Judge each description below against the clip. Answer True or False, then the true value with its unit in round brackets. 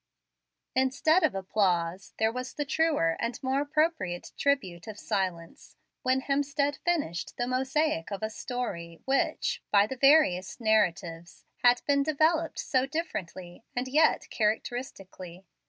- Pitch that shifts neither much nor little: False (7.1 semitones)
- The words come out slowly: True (130 wpm)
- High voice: True (245 Hz)